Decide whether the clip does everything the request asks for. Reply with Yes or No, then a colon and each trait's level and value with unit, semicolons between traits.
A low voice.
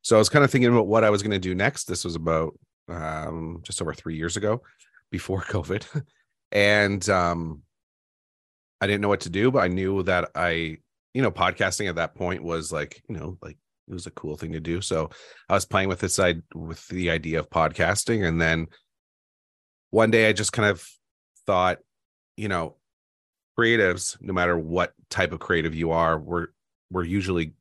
Yes: very low, 85 Hz